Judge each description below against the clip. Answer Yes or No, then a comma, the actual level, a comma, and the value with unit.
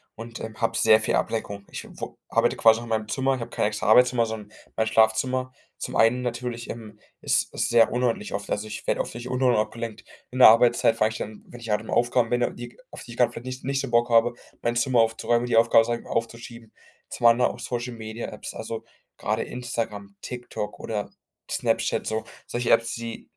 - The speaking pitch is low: Yes, low, 115 Hz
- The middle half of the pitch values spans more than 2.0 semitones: No, narrow, 1.7 semitones